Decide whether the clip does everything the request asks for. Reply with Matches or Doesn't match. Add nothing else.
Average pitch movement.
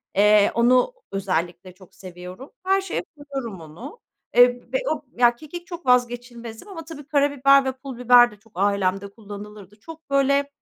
Doesn't match